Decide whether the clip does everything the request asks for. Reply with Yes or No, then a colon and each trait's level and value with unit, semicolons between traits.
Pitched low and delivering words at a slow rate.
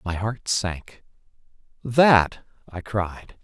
Yes: low, 105 Hz; slow, 105 wpm